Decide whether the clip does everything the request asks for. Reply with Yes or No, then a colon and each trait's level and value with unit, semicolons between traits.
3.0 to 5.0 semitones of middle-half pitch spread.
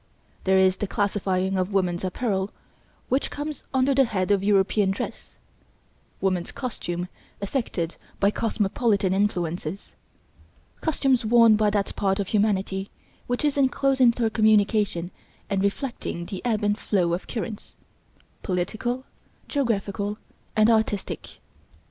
Yes: average, 3.4 semitones